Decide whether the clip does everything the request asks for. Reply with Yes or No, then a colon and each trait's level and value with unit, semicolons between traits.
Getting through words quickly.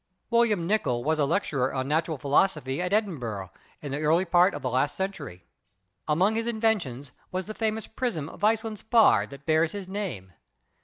No: average, 170 wpm